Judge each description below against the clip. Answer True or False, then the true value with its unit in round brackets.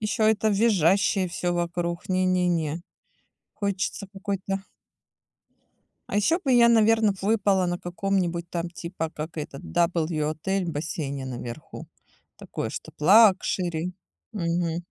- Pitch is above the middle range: False (180 Hz)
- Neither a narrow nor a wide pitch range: True (3.1 semitones)